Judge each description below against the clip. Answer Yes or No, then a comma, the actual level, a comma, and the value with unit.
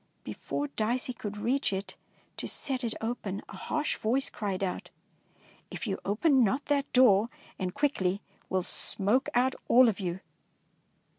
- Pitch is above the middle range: Yes, high, 225 Hz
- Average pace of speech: Yes, average, 160 wpm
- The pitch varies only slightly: No, average, 4.9 semitones